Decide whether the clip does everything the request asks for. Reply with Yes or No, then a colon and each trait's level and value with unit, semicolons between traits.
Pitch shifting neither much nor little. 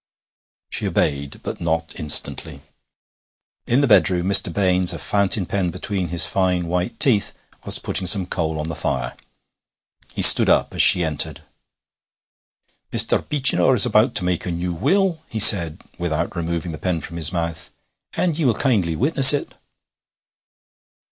Yes: average, 4.4 semitones